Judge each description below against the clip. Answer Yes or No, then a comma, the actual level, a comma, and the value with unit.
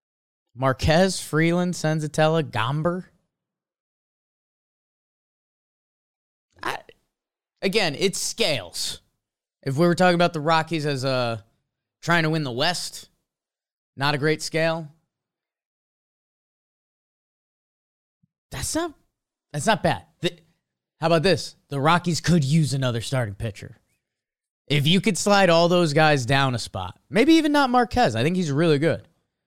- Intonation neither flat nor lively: Yes, average, 4.4 semitones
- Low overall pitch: No, medium, 160 Hz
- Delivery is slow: Yes, slow, 125 wpm